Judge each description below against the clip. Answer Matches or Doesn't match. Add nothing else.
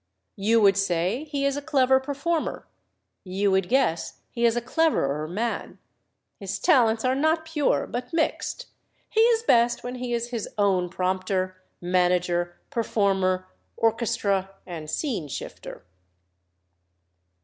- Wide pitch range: Matches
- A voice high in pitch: Matches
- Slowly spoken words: Matches